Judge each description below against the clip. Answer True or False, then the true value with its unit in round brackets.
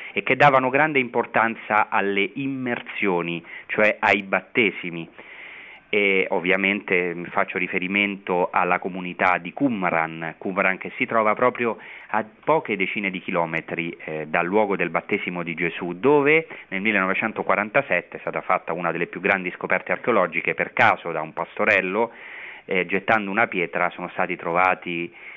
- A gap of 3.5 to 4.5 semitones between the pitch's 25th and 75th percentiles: True (3.9 semitones)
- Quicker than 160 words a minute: False (140 wpm)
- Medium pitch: False (95 Hz)